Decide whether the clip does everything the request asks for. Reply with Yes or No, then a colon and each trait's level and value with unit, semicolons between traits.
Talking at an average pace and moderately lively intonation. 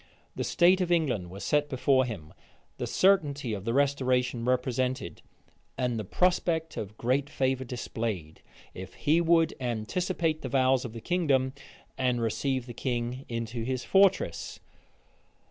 Yes: average, 145 wpm; average, 4.2 semitones